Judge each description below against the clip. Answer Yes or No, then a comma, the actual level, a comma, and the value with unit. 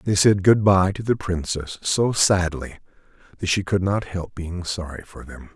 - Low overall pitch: Yes, very low, 90 Hz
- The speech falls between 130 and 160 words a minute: No, average, 195 wpm